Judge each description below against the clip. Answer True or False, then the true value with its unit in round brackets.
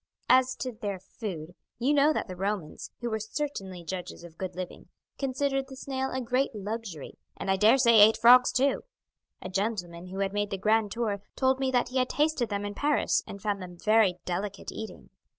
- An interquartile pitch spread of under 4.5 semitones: False (5.1 semitones)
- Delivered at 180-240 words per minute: True (205 wpm)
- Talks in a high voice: True (215 Hz)